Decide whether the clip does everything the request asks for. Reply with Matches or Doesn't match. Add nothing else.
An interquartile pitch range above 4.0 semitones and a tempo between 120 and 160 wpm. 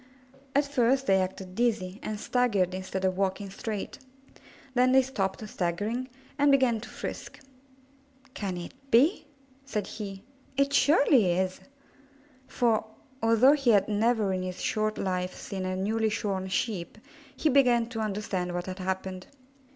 Matches